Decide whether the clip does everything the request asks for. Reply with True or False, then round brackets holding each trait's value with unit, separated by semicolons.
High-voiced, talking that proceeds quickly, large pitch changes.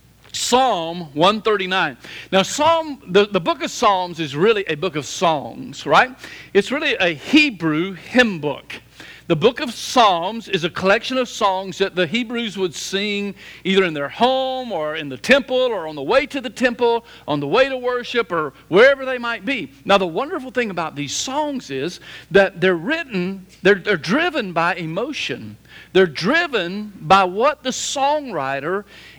False (200 Hz; 170 wpm; 6.4 semitones)